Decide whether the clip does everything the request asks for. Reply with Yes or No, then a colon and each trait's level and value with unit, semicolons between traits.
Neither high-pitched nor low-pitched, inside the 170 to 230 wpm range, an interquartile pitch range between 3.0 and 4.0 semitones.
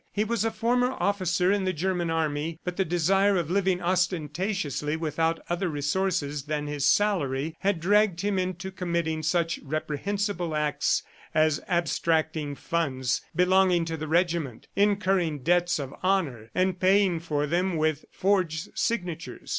No: medium, 170 Hz; average, 145 wpm; average, 3.5 semitones